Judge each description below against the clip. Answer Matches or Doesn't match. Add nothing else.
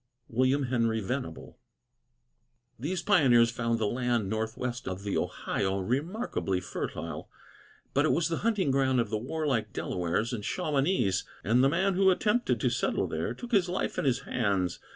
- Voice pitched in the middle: Doesn't match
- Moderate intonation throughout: Doesn't match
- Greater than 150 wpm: Matches